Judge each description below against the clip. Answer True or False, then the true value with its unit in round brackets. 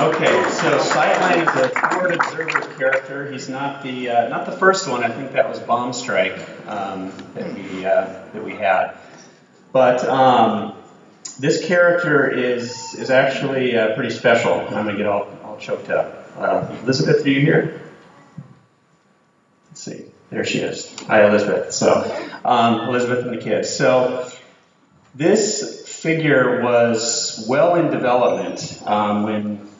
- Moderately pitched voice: False (125 Hz)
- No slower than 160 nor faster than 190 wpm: False (145 wpm)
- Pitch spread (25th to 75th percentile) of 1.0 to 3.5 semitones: True (3.2 semitones)